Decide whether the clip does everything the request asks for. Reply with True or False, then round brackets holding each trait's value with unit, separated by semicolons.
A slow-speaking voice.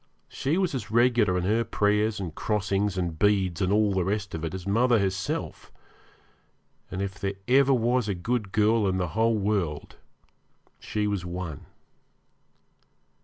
False (160 wpm)